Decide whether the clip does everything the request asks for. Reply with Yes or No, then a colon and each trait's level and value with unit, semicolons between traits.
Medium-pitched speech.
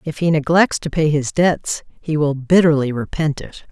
Yes: medium, 155 Hz